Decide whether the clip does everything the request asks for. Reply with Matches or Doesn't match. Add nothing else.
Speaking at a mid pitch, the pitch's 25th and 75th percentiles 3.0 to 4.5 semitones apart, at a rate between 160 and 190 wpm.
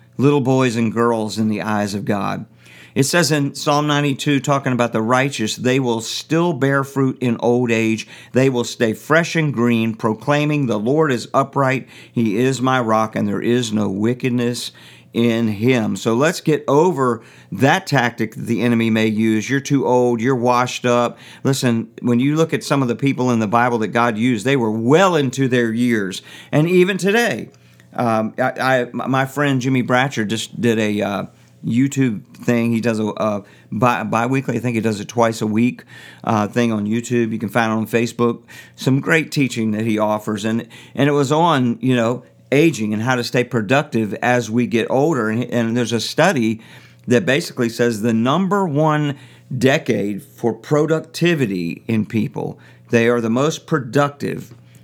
Doesn't match